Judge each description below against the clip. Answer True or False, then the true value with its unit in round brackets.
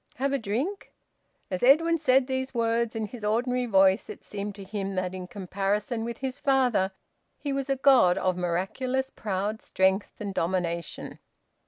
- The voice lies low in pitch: False (220 Hz)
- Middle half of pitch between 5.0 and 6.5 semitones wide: True (5.4 semitones)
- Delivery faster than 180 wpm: False (165 wpm)